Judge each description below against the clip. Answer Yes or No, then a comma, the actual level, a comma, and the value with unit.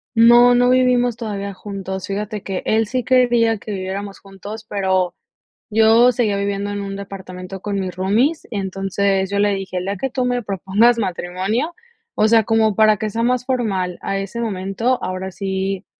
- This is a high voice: Yes, high, 205 Hz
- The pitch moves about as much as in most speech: Yes, average, 3.2 semitones